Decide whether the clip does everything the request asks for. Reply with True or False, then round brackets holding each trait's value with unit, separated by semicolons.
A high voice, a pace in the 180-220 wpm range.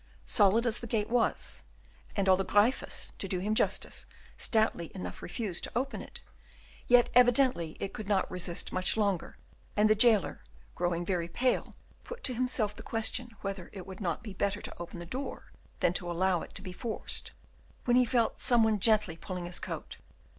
True (205 Hz; 185 wpm)